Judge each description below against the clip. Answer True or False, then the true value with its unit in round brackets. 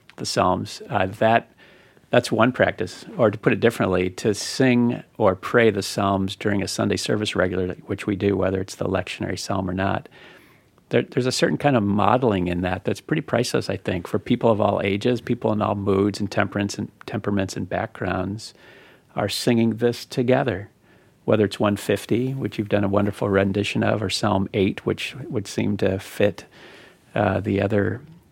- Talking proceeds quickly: False (180 wpm)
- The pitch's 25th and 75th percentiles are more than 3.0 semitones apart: False (2.7 semitones)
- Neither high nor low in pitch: False (105 Hz)